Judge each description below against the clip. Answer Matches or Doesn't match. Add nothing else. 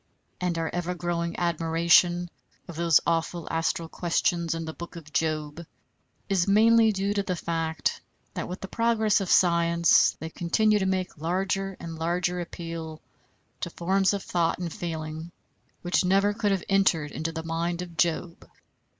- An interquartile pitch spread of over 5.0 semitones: Doesn't match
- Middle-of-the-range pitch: Matches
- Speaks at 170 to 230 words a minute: Doesn't match